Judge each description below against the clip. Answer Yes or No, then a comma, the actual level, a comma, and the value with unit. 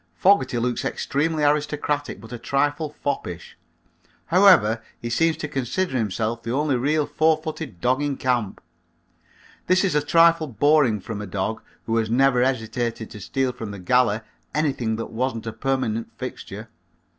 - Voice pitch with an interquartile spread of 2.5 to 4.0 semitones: No, average, 4.8 semitones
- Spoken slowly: No, average, 155 wpm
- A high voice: No, low, 130 Hz